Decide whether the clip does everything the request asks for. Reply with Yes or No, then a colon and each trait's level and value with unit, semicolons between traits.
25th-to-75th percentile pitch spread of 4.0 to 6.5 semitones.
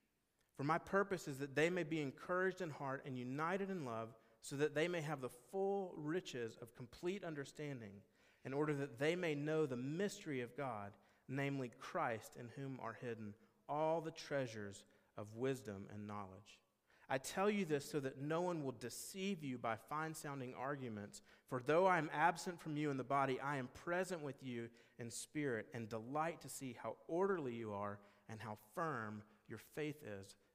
Yes: wide, 5.5 semitones